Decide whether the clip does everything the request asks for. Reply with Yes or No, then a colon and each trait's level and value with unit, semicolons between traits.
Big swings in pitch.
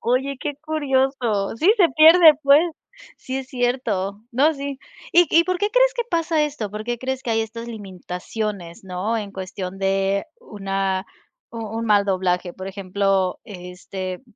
Yes: wide, 6.2 semitones